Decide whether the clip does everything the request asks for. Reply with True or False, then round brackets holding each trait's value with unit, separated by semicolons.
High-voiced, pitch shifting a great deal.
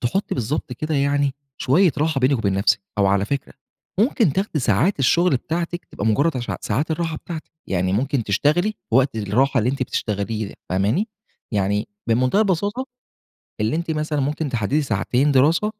False (140 Hz; 6.3 semitones)